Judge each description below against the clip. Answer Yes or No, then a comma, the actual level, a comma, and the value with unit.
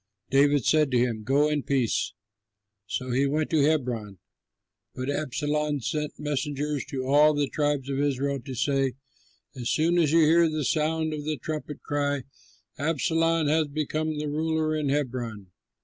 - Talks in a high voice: No, medium, 145 Hz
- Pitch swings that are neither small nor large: No, narrow, 2.3 semitones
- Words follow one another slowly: No, average, 155 wpm